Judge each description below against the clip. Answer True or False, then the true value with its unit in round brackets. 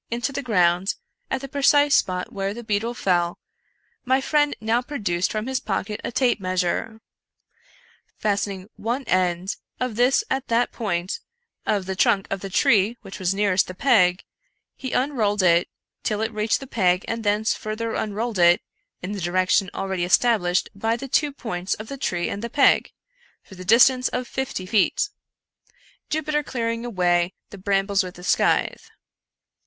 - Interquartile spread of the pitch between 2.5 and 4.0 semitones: False (4.7 semitones)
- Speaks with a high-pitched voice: True (210 Hz)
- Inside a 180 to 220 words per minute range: False (170 wpm)